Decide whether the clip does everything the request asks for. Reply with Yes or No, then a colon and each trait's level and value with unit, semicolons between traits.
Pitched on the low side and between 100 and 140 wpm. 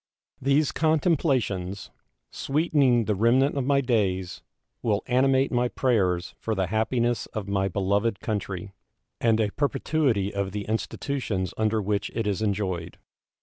Yes: low, 110 Hz; slow, 135 wpm